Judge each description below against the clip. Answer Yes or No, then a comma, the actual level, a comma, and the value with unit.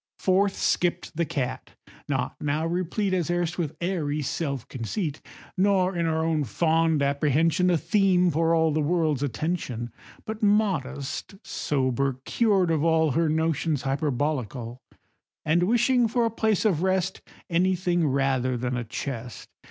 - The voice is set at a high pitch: No, medium, 160 Hz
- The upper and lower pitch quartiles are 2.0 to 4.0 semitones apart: No, average, 4.5 semitones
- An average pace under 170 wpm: Yes, average, 145 wpm